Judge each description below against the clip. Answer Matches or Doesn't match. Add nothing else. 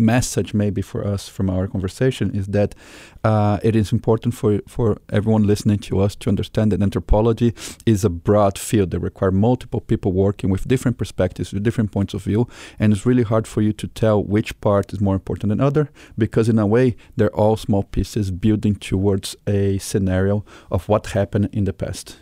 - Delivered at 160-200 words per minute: Matches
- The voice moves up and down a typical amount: Doesn't match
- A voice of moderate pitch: Doesn't match